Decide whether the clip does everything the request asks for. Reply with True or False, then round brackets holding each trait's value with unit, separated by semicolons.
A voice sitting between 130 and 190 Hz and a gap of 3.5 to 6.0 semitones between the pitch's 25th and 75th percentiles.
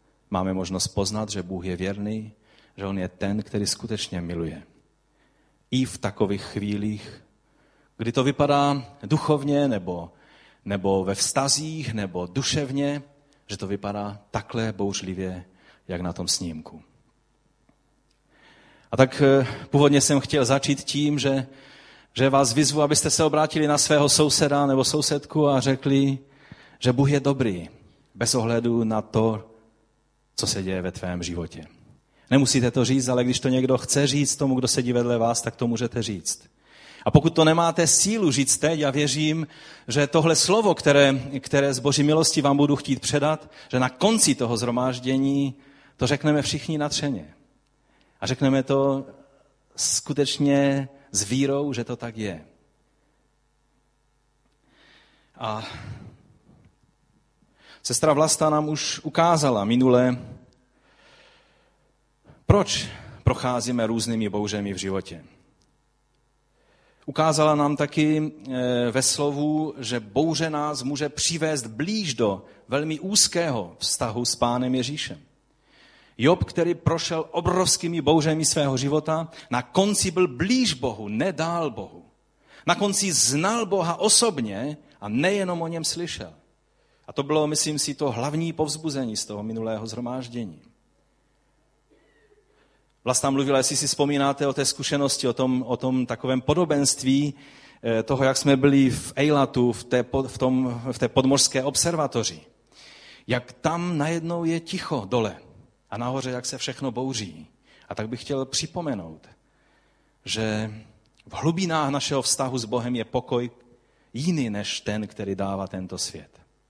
True (135 Hz; 4.2 semitones)